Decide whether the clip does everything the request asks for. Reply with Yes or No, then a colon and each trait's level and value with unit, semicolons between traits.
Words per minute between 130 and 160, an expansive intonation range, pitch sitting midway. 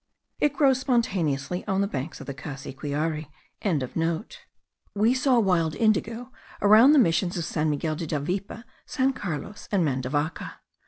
Yes: average, 140 wpm; wide, 7.1 semitones; medium, 180 Hz